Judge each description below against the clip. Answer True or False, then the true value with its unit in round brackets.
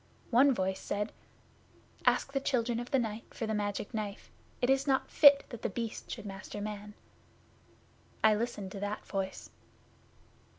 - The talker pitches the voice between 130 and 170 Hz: False (215 Hz)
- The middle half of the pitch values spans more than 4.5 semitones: False (3.2 semitones)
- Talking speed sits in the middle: True (160 wpm)